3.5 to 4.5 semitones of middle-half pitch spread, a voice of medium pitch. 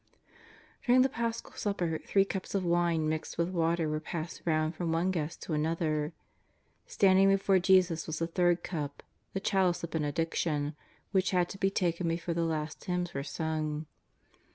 No: average, 3.0 semitones; medium, 170 Hz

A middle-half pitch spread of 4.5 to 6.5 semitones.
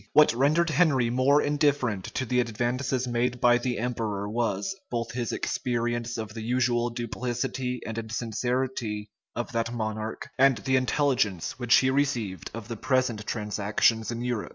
No: narrow, 2.5 semitones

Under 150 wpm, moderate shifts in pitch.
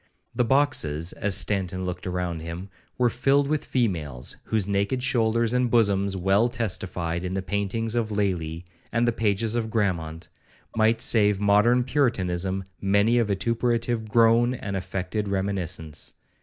Yes: average, 140 wpm; average, 3.9 semitones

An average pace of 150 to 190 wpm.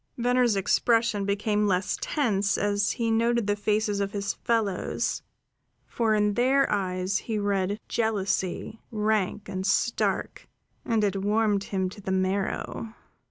No: slow, 135 wpm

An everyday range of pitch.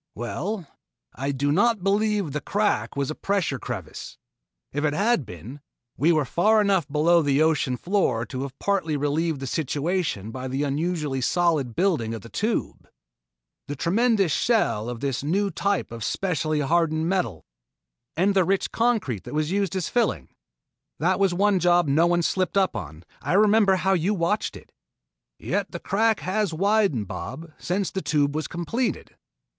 No: wide, 5.9 semitones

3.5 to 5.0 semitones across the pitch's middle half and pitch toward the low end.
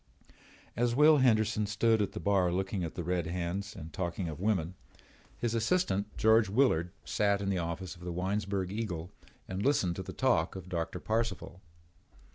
Yes: average, 3.8 semitones; very low, 95 Hz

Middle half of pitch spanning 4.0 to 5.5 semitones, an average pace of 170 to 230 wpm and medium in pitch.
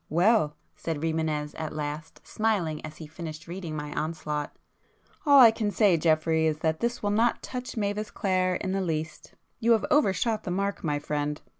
Yes: average, 5.0 semitones; average, 175 wpm; medium, 165 Hz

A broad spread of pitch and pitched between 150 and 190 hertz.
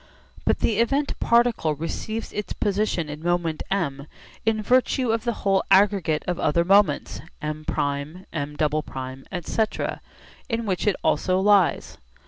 Yes: wide, 5.7 semitones; medium, 185 Hz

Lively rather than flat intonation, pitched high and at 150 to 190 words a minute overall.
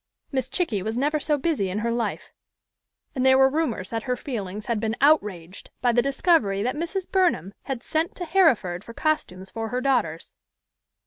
Yes: wide, 6.4 semitones; very high, 250 Hz; average, 185 wpm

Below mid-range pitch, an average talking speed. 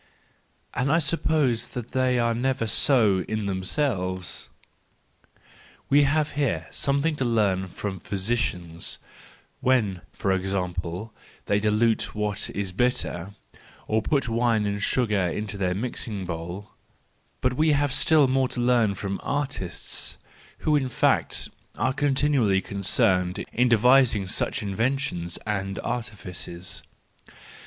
No: low, 110 Hz; slow, 125 wpm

